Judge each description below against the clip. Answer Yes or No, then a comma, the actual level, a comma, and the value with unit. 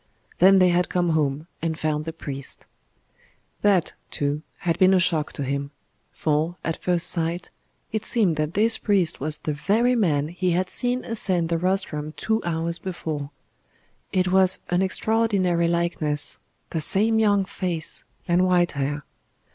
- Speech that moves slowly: No, average, 155 wpm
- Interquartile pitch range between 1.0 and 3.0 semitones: No, average, 3.5 semitones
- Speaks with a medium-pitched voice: Yes, medium, 175 Hz